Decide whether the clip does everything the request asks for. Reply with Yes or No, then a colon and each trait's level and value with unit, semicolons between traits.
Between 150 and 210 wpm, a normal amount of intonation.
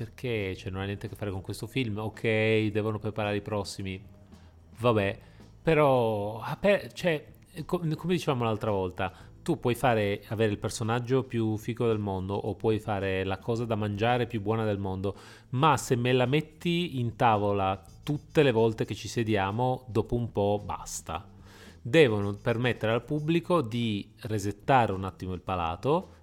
Yes: average, 160 wpm; average, 3.3 semitones